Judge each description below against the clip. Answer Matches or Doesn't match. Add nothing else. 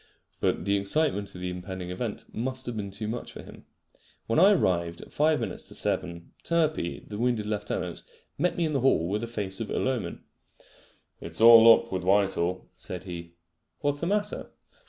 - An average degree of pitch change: Doesn't match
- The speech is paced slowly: Doesn't match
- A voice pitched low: Matches